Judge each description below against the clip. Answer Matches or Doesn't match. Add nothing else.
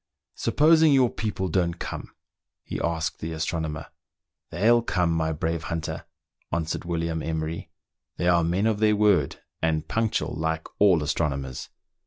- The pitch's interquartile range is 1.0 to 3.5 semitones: Doesn't match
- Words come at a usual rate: Matches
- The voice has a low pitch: Matches